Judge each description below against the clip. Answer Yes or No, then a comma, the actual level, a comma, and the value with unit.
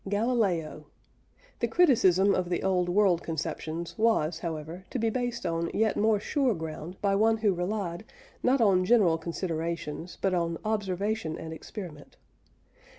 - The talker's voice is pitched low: No, medium, 185 Hz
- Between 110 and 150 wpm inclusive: Yes, average, 145 wpm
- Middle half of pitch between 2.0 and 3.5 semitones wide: No, average, 4.5 semitones